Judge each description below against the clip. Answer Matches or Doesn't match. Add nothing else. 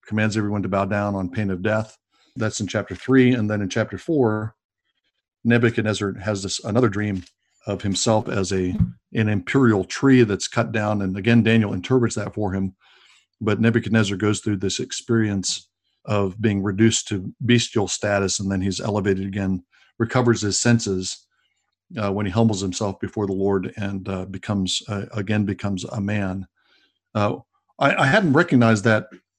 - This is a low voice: Matches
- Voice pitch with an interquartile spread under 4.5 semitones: Matches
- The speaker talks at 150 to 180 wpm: Matches